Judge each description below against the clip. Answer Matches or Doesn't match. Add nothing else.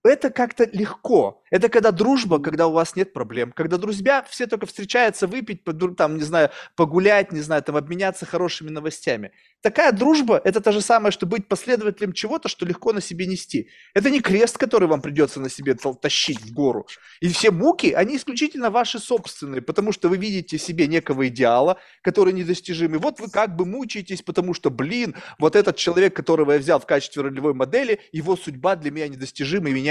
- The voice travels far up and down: Matches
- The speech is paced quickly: Matches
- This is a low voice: Doesn't match